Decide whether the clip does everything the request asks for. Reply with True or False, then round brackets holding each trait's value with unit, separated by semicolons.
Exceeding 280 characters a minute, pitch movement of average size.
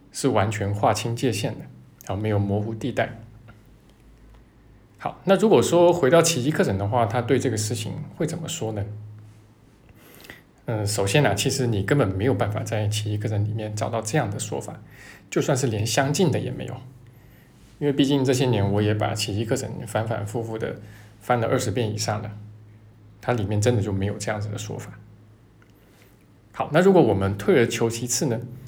False (275 characters per minute; 3.4 semitones)